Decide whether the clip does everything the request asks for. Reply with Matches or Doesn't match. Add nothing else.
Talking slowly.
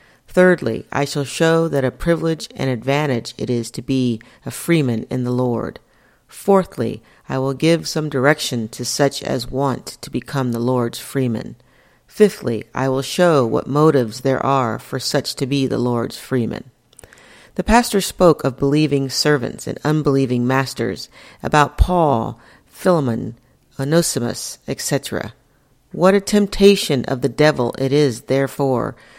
Doesn't match